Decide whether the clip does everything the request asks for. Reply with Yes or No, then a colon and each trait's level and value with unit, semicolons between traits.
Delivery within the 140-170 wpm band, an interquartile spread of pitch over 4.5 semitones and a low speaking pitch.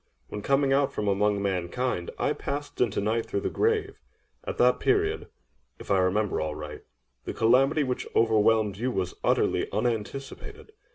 Yes: average, 150 wpm; wide, 5.5 semitones; low, 115 Hz